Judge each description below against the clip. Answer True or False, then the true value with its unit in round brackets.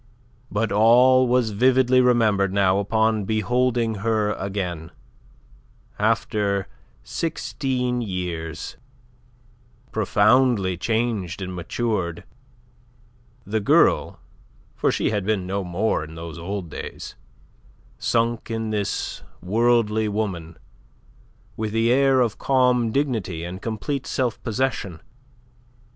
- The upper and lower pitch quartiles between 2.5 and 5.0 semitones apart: True (3.9 semitones)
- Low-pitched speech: True (110 Hz)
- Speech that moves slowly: True (100 wpm)